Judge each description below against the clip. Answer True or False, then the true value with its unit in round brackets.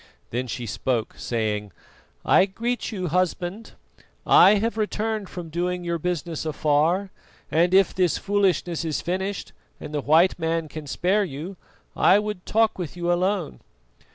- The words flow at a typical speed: True (150 wpm)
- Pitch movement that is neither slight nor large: True (4.0 semitones)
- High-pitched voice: False (175 Hz)